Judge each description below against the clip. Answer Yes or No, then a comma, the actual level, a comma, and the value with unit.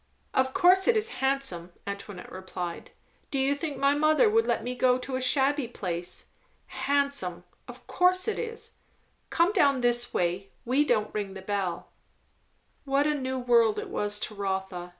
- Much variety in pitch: Yes, wide, 6.5 semitones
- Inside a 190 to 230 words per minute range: No, average, 170 wpm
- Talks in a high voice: Yes, very high, 255 Hz